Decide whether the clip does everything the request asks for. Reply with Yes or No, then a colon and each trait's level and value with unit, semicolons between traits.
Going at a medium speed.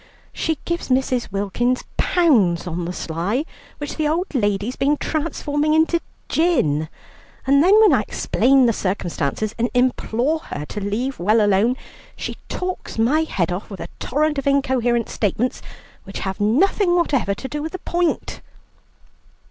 Yes: average, 155 wpm